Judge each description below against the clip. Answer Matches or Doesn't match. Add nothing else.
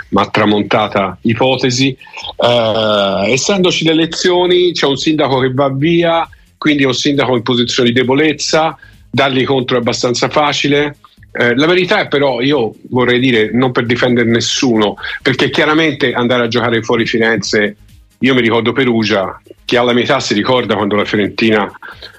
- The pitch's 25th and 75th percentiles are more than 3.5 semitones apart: Matches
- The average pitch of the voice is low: Matches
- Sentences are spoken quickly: Doesn't match